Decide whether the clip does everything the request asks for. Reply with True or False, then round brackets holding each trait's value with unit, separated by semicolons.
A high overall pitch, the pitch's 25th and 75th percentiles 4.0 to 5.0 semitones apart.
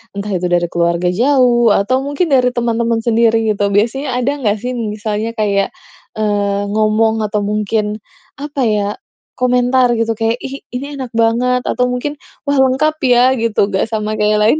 False (225 Hz; 3.1 semitones)